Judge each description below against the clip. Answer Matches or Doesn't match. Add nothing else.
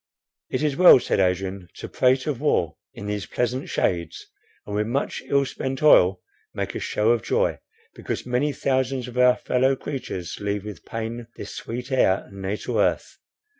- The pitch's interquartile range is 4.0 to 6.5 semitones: Matches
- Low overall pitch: Matches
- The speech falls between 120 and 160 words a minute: Doesn't match